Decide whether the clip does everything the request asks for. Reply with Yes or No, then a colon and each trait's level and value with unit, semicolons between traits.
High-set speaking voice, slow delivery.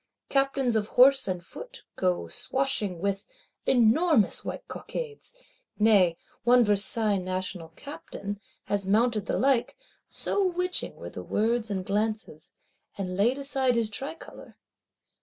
Yes: high, 220 Hz; slow, 125 wpm